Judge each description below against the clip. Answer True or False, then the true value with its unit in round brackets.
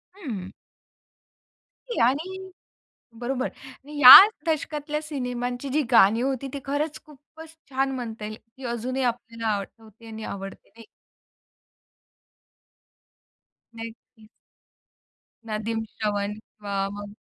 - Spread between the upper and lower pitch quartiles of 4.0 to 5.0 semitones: True (4.3 semitones)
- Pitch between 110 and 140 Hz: False (245 Hz)